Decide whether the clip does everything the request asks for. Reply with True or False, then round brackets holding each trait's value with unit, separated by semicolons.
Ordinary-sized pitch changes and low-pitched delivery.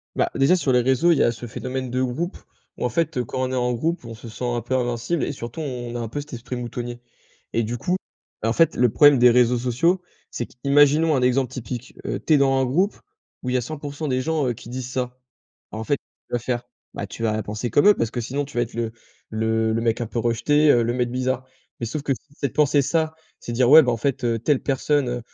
True (3.2 semitones; 125 Hz)